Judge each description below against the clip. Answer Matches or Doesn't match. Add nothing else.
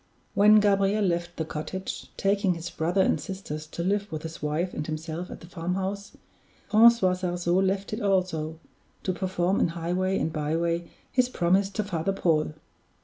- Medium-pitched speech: Matches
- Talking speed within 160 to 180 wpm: Matches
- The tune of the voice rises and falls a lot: Doesn't match